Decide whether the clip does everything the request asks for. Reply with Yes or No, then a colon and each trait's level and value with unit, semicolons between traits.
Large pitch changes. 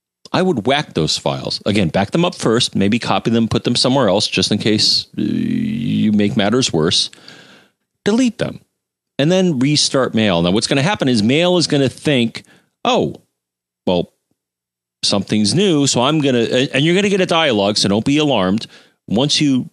Yes: wide, 6.1 semitones